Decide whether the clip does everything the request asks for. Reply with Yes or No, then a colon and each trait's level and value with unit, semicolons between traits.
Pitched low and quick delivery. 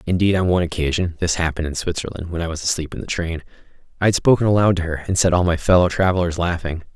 Yes: very low, 85 Hz; fast, 240 wpm